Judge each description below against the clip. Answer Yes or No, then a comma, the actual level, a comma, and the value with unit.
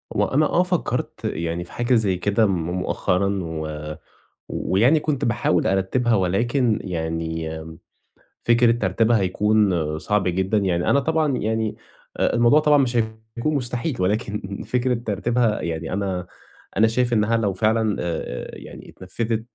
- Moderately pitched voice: No, low, 105 Hz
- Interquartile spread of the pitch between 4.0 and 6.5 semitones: Yes, average, 4.6 semitones